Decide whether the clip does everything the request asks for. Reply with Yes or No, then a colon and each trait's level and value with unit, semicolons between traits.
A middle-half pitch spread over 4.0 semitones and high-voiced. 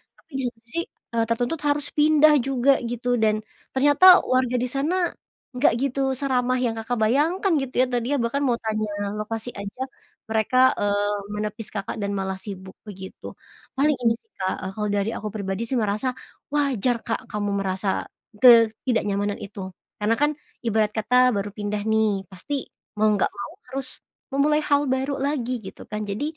Yes: average, 4.5 semitones; high, 230 Hz